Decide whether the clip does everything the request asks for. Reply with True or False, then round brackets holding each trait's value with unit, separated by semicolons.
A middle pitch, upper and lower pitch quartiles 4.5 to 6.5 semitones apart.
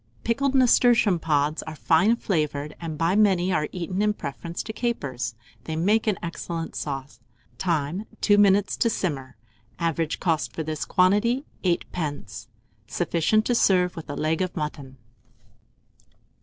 True (170 Hz; 5.2 semitones)